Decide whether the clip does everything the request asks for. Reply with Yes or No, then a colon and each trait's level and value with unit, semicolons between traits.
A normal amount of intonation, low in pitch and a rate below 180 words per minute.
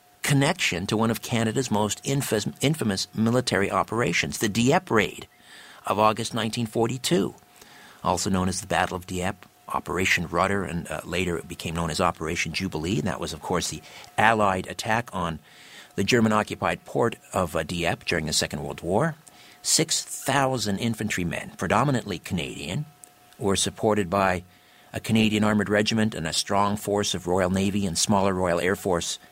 Yes: average, 3.5 semitones; low, 100 Hz; average, 160 wpm